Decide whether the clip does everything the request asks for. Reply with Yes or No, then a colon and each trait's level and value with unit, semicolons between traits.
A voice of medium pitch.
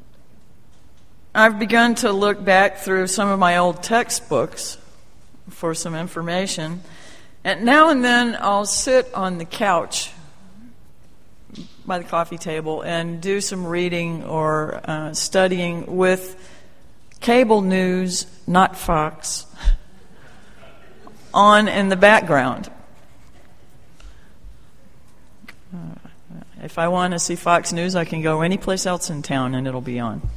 Yes: medium, 180 Hz